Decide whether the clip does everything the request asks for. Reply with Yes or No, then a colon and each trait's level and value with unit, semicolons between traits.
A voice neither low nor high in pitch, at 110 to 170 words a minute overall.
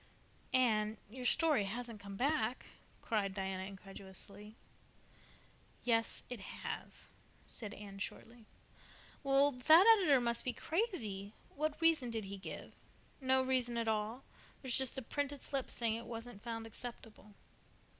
No: high, 235 Hz; average, 140 wpm